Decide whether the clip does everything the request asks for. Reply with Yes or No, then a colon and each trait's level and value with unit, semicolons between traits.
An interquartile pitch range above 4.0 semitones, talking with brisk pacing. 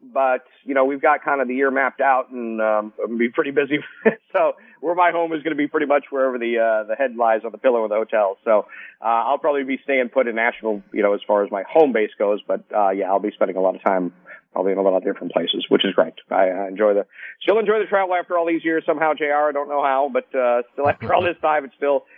Yes: wide, 5.5 semitones; fast, 280 wpm